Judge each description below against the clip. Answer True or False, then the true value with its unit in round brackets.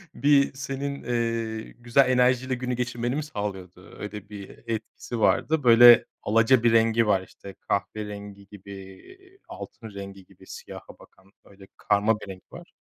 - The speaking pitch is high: False (115 Hz)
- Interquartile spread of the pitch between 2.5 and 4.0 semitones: True (3.7 semitones)